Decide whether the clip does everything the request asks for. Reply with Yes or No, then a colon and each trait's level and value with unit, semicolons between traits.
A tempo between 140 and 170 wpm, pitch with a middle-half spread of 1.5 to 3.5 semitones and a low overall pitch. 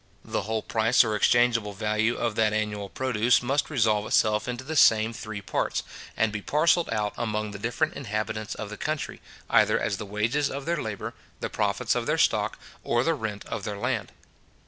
No: average, 190 wpm; average, 2.7 semitones; low, 110 Hz